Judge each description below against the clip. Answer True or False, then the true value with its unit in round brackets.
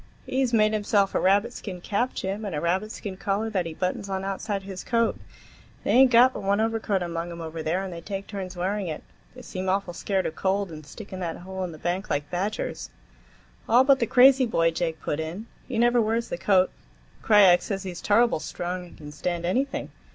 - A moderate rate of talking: False (220 wpm)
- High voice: True (195 Hz)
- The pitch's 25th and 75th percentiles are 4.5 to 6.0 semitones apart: False (3.6 semitones)